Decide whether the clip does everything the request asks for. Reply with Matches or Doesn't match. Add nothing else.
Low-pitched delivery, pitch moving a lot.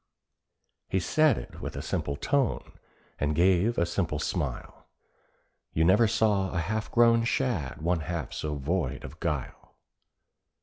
Matches